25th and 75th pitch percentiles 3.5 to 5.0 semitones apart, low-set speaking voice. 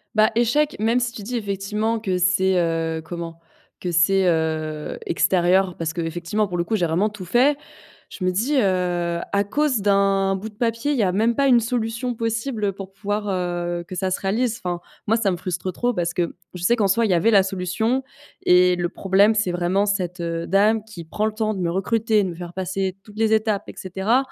No: average, 3.8 semitones; high, 195 Hz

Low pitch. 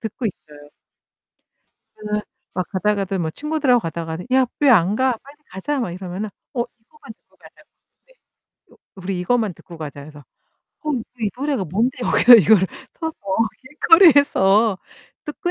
No: high, 215 Hz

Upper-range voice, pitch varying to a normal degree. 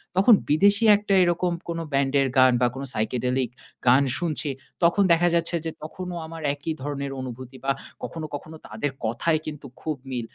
No: medium, 150 Hz; average, 4.2 semitones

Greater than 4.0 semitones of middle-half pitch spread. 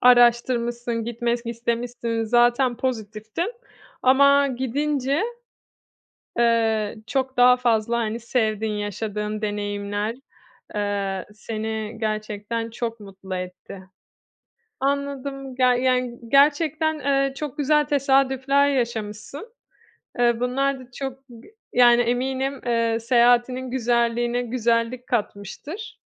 No: average, 3.2 semitones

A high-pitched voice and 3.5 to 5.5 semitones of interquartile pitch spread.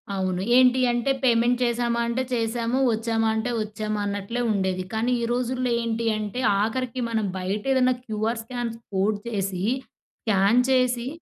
No: high, 230 Hz; narrow, 2.6 semitones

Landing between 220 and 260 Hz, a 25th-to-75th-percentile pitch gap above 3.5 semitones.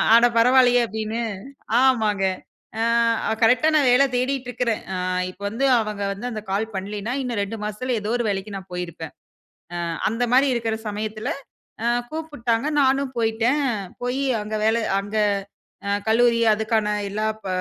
No: high, 225 Hz; average, 2.9 semitones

